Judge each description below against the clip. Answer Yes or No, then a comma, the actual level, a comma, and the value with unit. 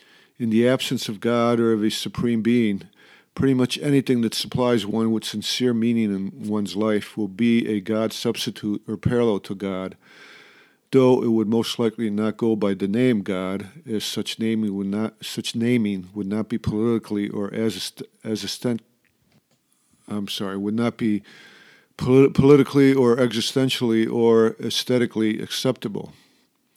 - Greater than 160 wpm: No, average, 155 wpm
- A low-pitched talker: Yes, low, 115 Hz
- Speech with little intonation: Yes, narrow, 2.2 semitones